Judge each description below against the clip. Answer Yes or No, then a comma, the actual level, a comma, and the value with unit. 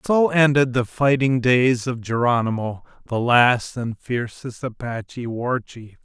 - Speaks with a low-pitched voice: Yes, low, 125 Hz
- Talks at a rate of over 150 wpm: No, average, 140 wpm